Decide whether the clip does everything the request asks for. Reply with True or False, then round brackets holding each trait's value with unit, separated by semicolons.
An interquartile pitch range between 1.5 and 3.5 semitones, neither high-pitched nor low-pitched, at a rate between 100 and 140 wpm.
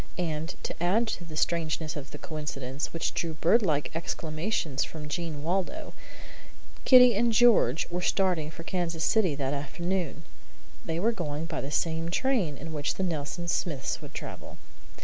False (3.2 semitones; 165 Hz; 160 wpm)